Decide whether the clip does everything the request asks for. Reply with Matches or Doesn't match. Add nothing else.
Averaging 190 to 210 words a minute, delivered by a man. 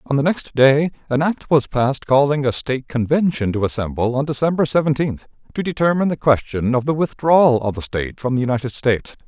Matches